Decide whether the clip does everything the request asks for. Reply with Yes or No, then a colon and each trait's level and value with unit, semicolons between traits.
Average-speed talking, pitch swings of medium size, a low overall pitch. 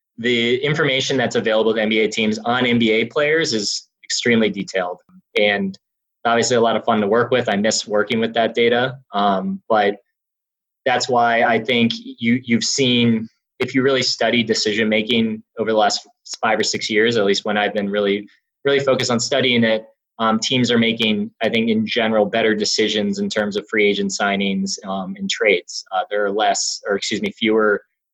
Yes: average, 190 wpm; average, 3.7 semitones; low, 115 Hz